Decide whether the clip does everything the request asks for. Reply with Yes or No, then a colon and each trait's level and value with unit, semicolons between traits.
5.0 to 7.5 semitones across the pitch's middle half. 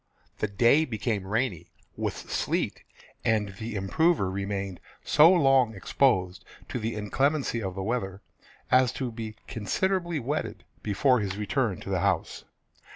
Yes: average, 5.3 semitones